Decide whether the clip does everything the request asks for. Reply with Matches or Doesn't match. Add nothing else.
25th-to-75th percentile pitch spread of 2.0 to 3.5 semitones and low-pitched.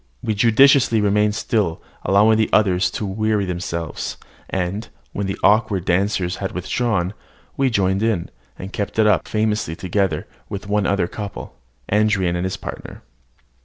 Matches